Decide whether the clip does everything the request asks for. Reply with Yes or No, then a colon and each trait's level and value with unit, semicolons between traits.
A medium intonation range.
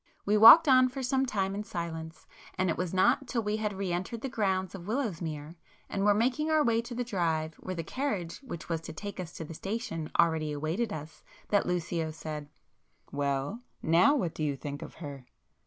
No: wide, 6.2 semitones